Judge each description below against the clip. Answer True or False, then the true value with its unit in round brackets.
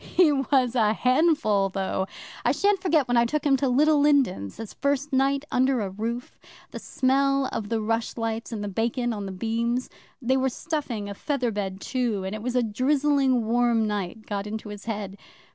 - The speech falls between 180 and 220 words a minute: True (195 wpm)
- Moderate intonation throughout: True (4.4 semitones)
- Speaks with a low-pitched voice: False (240 Hz)